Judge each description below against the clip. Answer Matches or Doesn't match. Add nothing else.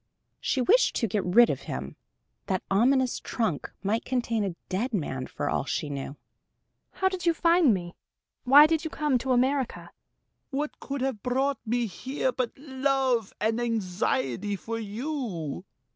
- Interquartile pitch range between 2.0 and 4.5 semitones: Doesn't match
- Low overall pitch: Doesn't match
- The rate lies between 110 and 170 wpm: Matches